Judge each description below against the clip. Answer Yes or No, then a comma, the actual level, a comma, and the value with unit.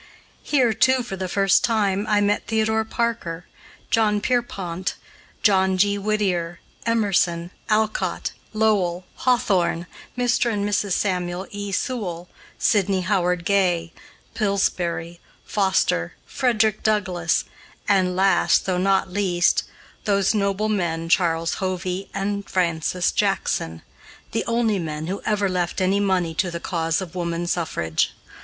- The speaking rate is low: Yes, slow, 125 wpm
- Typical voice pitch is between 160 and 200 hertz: Yes, high, 190 Hz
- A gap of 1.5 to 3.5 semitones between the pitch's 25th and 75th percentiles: Yes, average, 3.2 semitones